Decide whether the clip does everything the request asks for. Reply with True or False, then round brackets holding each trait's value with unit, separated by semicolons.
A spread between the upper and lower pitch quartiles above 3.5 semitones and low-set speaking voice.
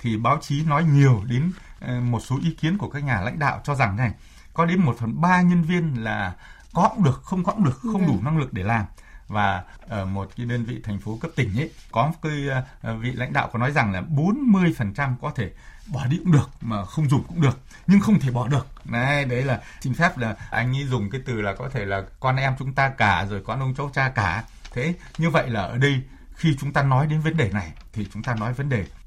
True (5.1 semitones; 130 Hz)